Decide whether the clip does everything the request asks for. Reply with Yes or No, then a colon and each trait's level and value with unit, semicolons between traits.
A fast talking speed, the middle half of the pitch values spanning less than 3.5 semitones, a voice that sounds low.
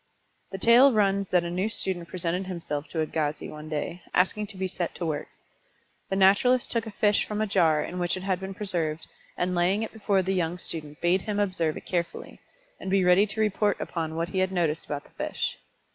No: fast, 220 wpm; average, 2.9 semitones; medium, 185 Hz